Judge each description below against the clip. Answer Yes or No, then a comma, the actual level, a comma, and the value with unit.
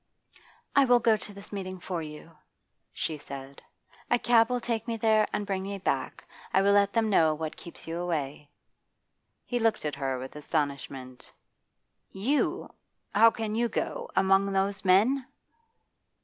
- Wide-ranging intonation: Yes, wide, 6.2 semitones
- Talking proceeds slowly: No, average, 160 wpm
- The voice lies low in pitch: No, high, 195 Hz